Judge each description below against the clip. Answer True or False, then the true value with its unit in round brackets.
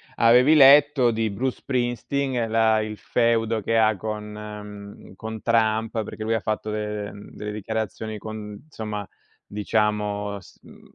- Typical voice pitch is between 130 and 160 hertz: False (110 Hz)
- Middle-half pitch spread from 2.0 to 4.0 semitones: False (1.6 semitones)